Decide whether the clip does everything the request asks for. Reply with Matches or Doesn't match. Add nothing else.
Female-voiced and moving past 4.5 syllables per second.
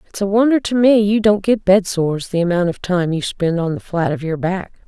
Matches